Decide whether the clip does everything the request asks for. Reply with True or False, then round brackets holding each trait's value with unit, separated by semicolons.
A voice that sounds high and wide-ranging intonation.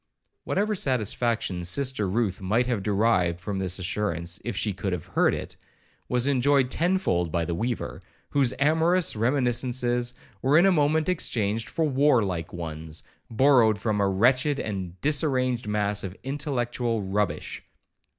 False (115 Hz; 5.9 semitones)